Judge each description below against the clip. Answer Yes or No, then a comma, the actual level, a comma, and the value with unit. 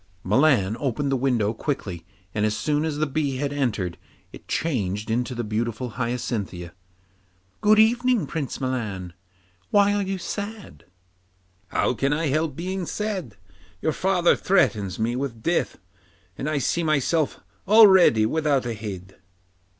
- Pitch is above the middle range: No, low, 135 Hz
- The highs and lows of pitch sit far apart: Yes, wide, 7.0 semitones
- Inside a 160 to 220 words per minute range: No, average, 145 wpm